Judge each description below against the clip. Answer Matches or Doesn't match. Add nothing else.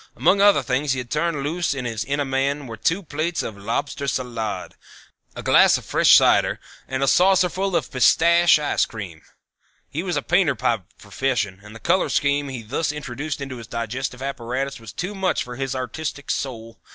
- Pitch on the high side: Doesn't match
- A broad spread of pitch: Doesn't match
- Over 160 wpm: Matches